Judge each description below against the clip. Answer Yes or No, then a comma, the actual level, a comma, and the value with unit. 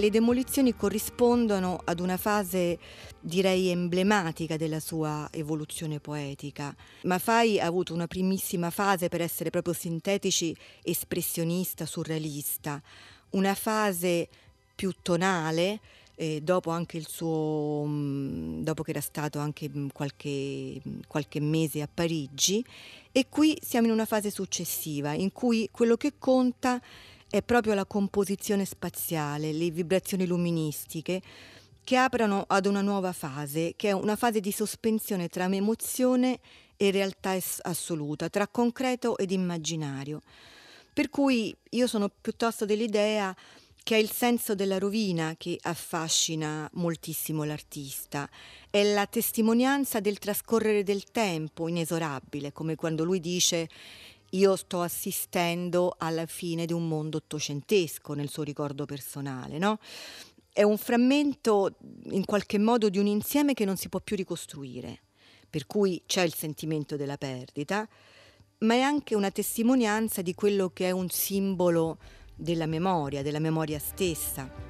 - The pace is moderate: Yes, average, 130 wpm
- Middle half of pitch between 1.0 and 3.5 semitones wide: No, average, 5.0 semitones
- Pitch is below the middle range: No, medium, 180 Hz